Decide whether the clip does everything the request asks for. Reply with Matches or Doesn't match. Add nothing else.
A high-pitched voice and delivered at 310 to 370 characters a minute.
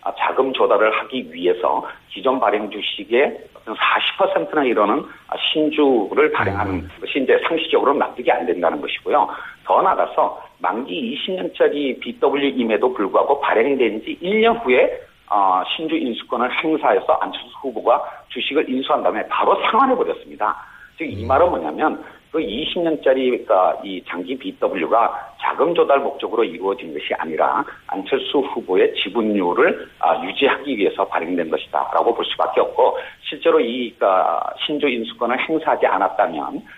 Matches